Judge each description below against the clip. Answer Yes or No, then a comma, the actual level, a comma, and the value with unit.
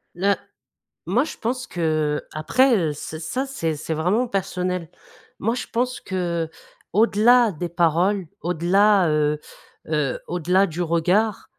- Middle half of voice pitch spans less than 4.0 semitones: No, average, 4.6 semitones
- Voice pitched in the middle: Yes, medium, 180 Hz